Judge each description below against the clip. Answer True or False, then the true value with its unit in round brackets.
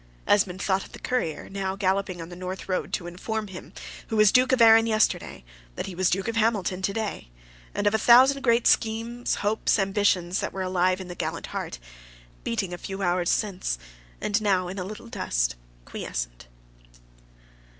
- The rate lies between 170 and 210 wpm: True (185 wpm)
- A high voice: True (195 Hz)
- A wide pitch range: False (3.3 semitones)